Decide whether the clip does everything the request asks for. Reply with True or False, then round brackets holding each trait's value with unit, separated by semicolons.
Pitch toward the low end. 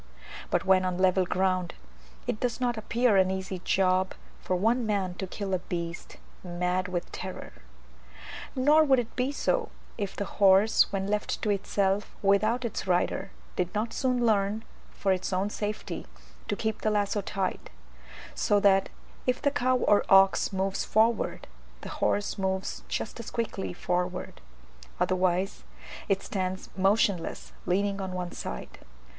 False (195 Hz)